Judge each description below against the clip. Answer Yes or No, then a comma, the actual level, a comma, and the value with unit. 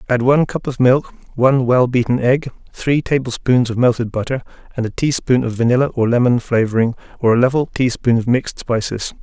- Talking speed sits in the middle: Yes, average, 190 wpm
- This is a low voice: Yes, low, 125 Hz